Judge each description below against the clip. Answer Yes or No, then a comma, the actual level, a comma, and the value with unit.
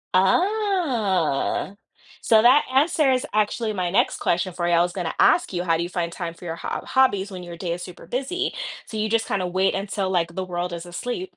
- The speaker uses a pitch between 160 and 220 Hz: Yes, high, 190 Hz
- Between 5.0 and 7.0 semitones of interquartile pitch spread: Yes, wide, 5.6 semitones